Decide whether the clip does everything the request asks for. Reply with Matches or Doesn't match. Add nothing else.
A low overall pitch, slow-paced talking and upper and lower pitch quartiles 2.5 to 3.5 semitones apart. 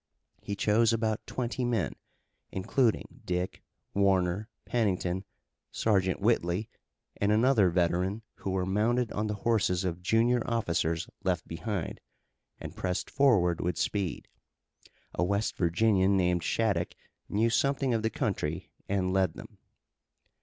Doesn't match